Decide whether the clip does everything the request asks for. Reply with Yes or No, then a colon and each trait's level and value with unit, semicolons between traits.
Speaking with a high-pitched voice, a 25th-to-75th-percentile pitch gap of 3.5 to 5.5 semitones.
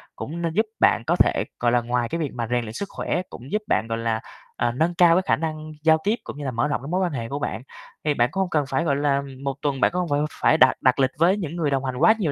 No: medium, 145 Hz; average, 5.1 semitones